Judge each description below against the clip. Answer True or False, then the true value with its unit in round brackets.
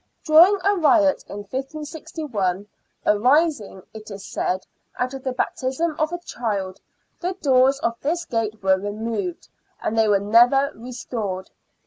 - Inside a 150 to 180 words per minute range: False (140 wpm)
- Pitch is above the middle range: True (250 Hz)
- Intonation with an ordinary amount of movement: False (6.8 semitones)